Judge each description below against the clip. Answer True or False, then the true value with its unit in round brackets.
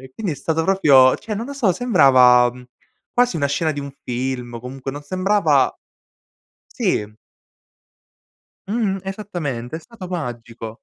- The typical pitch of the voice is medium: True (145 Hz)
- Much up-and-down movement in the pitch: True (7.3 semitones)